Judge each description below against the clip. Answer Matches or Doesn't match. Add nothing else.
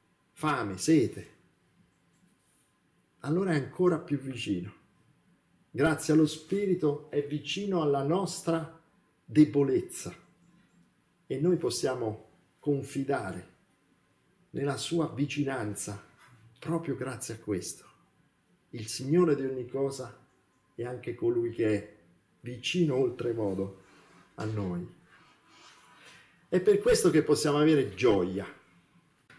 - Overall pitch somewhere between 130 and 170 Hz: Matches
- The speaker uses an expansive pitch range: Matches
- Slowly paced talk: Matches